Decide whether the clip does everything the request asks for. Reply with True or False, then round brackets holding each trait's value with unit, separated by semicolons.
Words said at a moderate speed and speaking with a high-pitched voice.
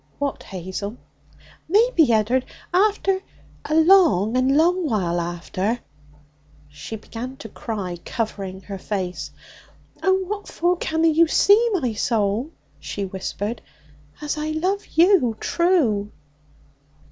False (120 wpm; 245 Hz)